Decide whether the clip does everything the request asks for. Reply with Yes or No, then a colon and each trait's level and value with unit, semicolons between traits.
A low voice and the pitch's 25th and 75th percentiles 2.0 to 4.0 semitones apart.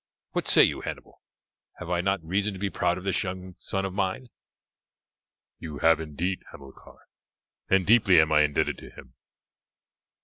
Yes: very low, 90 Hz; average, 3.2 semitones